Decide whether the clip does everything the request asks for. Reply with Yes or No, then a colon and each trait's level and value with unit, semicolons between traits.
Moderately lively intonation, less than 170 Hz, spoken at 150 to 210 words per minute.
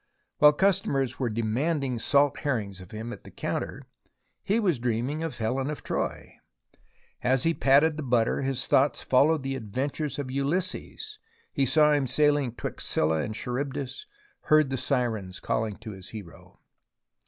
Yes: average, 4.3 semitones; low, 135 Hz; average, 155 wpm